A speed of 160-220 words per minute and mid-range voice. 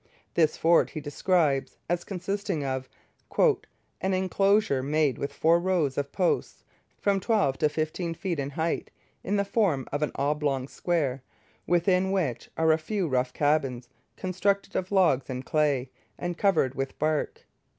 No: average, 150 wpm; medium, 160 Hz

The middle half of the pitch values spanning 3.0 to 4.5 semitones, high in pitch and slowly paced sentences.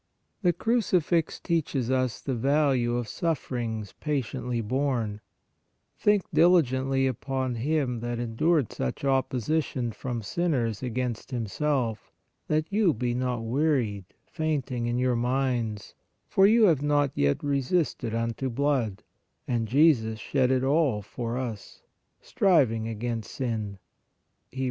No: average, 4.1 semitones; low, 130 Hz; slow, 125 wpm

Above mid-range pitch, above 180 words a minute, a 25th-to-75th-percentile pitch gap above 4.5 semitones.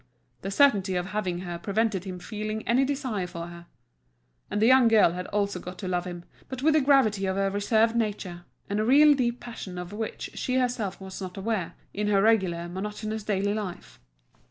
No: high, 205 Hz; average, 200 wpm; average, 3.6 semitones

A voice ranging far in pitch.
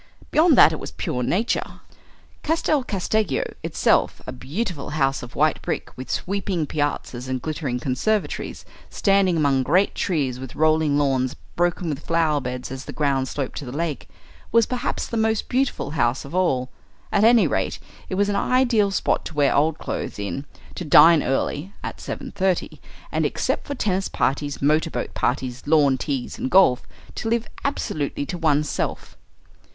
Yes: wide, 6.5 semitones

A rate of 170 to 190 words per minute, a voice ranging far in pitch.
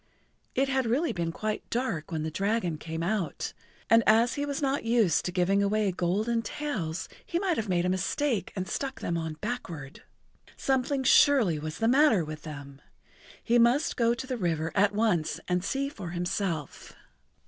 Yes: average, 180 wpm; wide, 6.4 semitones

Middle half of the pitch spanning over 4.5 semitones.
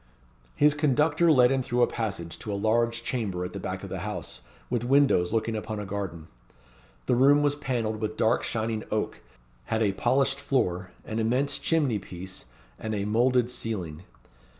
No: average, 4.0 semitones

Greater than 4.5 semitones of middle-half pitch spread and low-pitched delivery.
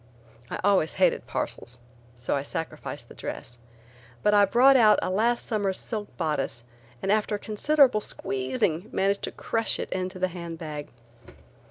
No: average, 5.3 semitones; high, 190 Hz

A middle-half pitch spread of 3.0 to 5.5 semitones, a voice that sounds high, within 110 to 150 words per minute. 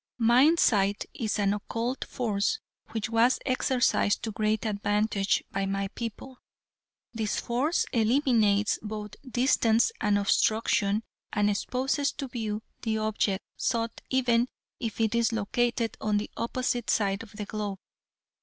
No: narrow, 2.6 semitones; high, 220 Hz; slow, 135 wpm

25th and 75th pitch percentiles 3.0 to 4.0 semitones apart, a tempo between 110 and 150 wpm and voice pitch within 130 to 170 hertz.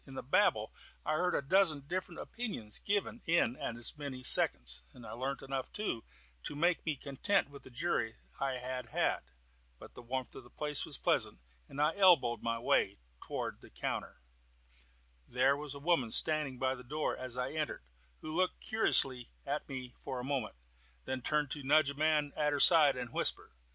No: average, 3.6 semitones; average, 190 wpm; medium, 140 Hz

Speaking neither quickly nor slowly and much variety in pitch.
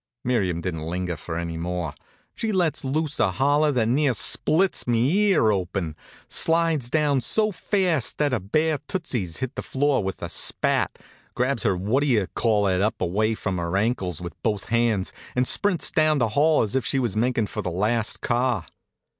Yes: average, 185 wpm; wide, 7.5 semitones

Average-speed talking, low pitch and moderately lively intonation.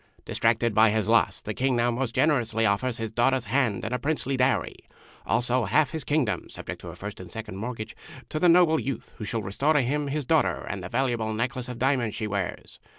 No: fast, 215 wpm; low, 120 Hz; average, 3.6 semitones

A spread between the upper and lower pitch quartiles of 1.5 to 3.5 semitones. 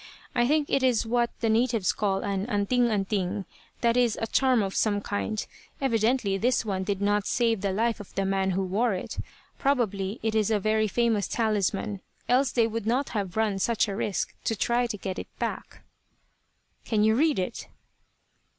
Yes: average, 3.1 semitones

